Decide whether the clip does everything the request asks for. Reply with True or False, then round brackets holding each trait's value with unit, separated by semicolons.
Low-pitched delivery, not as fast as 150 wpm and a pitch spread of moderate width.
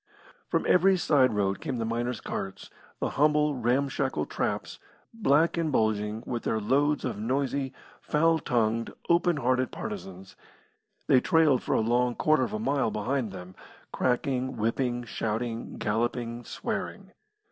True (125 Hz; 140 wpm; 4.1 semitones)